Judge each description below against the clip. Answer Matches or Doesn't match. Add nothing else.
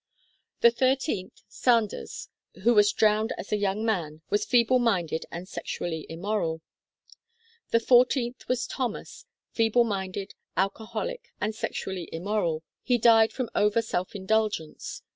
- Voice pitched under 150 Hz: Doesn't match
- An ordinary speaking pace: Doesn't match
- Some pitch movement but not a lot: Matches